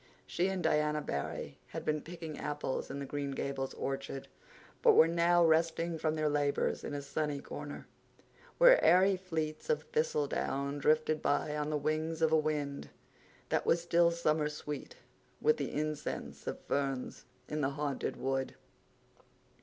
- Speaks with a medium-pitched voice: Yes, medium, 155 Hz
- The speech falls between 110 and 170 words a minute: Yes, average, 155 wpm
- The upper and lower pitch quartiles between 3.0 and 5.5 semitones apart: No, narrow, 2.6 semitones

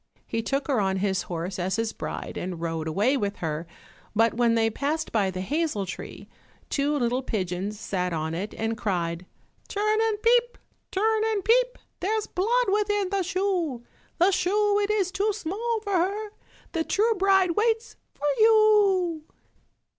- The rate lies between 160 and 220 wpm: Yes, average, 165 wpm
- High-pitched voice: Yes, very high, 325 Hz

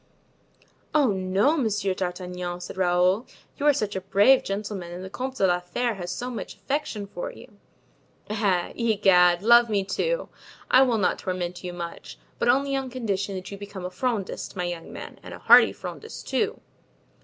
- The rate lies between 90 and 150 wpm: No, average, 180 wpm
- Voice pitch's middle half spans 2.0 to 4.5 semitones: No, average, 5.0 semitones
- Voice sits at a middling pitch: No, high, 200 Hz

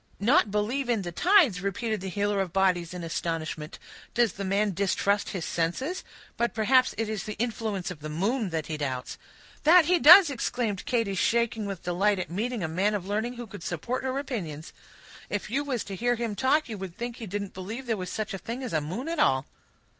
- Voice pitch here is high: Yes, high, 205 Hz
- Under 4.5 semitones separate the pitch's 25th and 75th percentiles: No, average, 4.9 semitones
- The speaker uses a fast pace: Yes, fast, 220 wpm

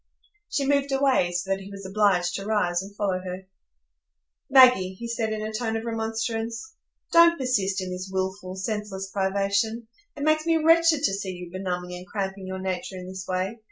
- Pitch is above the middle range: Yes, high, 200 Hz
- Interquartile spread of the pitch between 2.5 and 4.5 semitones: Yes, average, 3.8 semitones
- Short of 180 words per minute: No, average, 190 wpm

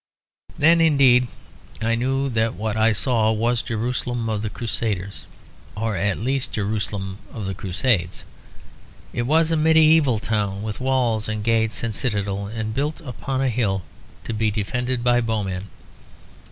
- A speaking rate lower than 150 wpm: No, average, 155 wpm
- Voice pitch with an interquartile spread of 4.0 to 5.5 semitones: No, average, 3.3 semitones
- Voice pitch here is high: No, low, 115 Hz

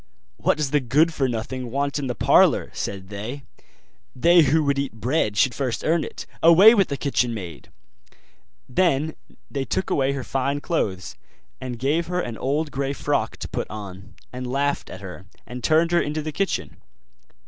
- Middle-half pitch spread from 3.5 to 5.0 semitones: Yes, average, 4.5 semitones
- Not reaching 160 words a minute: No, average, 180 wpm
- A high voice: No, low, 135 Hz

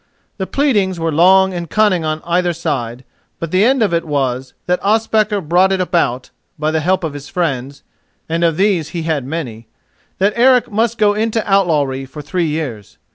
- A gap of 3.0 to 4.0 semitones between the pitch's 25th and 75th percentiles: No, average, 4.9 semitones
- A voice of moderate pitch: Yes, medium, 170 Hz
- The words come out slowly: No, average, 180 wpm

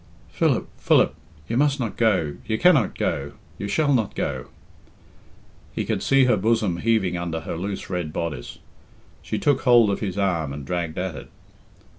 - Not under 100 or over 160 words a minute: No, average, 170 wpm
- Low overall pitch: Yes, low, 100 Hz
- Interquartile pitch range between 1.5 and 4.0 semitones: No, wide, 5.6 semitones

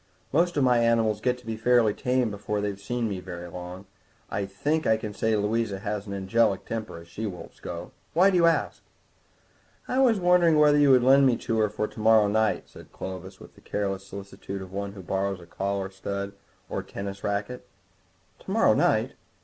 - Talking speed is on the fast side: Yes, fast, 210 wpm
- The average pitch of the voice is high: No, low, 105 Hz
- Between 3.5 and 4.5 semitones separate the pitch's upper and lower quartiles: Yes, average, 4.1 semitones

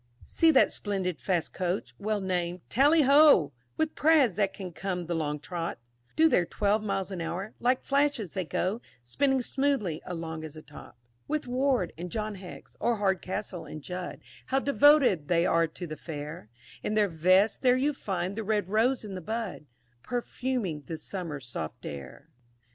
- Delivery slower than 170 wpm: No, average, 175 wpm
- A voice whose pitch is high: Yes, high, 195 Hz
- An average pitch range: No, wide, 6.6 semitones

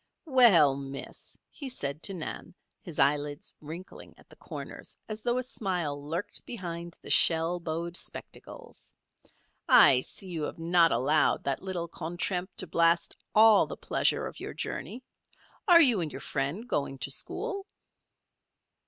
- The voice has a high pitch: No, medium, 170 Hz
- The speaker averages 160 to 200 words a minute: No, average, 150 wpm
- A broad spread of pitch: Yes, wide, 6.0 semitones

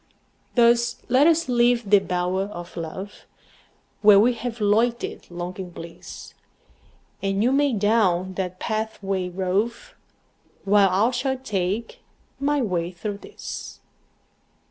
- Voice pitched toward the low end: No, high, 205 Hz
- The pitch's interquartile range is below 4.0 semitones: No, average, 4.4 semitones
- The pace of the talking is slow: Yes, slow, 120 wpm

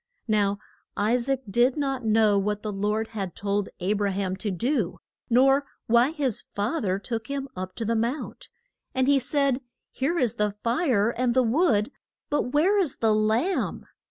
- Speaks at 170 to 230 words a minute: Yes, average, 180 wpm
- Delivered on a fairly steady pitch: No, average, 4.6 semitones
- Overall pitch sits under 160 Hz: No, high, 230 Hz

